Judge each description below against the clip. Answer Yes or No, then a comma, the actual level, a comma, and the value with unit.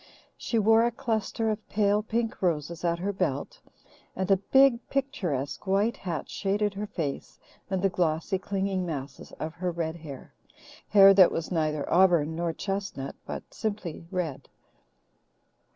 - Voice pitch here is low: No, high, 190 Hz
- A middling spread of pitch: Yes, average, 4.1 semitones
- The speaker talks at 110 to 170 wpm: Yes, average, 150 wpm